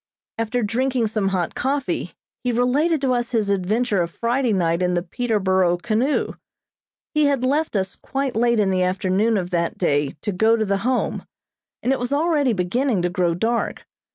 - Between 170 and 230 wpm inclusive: Yes, average, 180 wpm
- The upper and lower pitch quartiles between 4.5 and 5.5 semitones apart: Yes, average, 5.2 semitones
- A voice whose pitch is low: No, high, 220 Hz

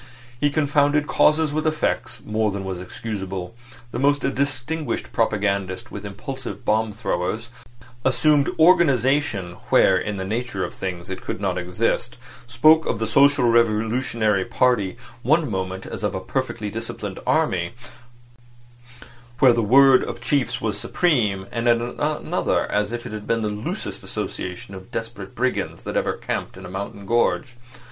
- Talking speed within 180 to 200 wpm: No, average, 155 wpm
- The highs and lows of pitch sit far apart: Yes, wide, 5.7 semitones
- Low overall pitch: Yes, low, 115 Hz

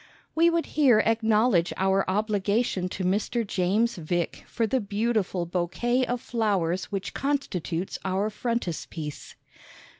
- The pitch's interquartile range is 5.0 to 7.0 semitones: No, average, 4.4 semitones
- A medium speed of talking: No, slow, 120 wpm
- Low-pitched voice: No, high, 205 Hz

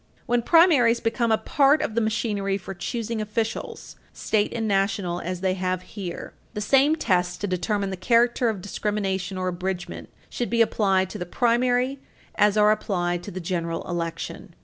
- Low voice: No, high, 205 Hz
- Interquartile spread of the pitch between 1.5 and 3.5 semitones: No, average, 4.1 semitones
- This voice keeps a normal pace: Yes, average, 170 wpm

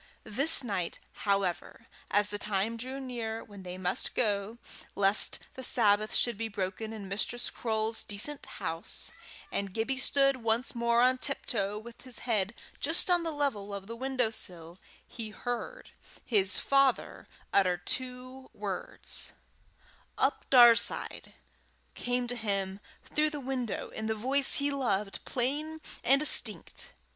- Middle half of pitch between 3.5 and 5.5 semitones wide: Yes, average, 4.3 semitones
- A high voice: Yes, high, 230 Hz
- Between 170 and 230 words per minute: No, average, 140 wpm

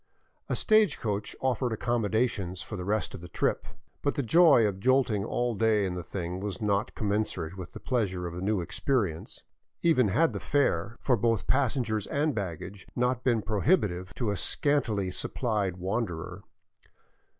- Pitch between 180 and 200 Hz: No, low, 105 Hz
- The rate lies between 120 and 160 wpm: No, average, 170 wpm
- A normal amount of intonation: Yes, average, 4.8 semitones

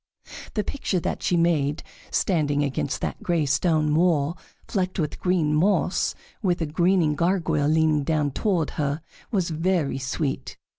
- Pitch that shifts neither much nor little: Yes, average, 3.3 semitones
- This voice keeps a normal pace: Yes, average, 145 wpm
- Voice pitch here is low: No, medium, 160 Hz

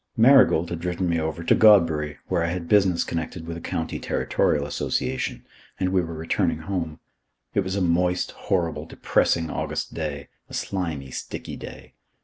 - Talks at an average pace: Yes, average, 165 wpm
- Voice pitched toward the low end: Yes, very low, 85 Hz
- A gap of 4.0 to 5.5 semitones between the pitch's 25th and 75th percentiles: No, narrow, 2.5 semitones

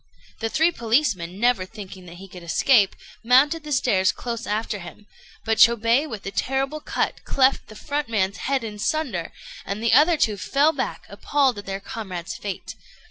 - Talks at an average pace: Yes, average, 180 wpm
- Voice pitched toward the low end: No, high, 225 Hz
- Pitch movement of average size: No, wide, 5.7 semitones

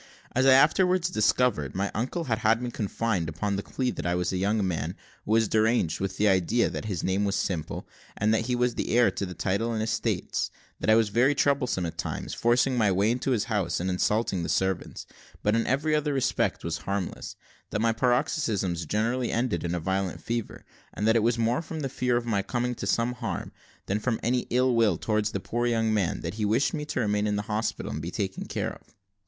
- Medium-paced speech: No, fast, 230 wpm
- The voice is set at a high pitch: No, low, 110 Hz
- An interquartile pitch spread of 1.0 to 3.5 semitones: No, average, 4.0 semitones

